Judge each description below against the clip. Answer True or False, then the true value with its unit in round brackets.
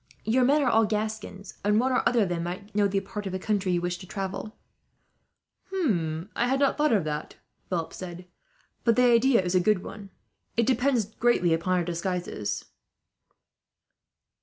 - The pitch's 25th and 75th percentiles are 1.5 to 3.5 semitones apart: False (4.6 semitones)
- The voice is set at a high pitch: True (205 Hz)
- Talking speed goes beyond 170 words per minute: True (185 wpm)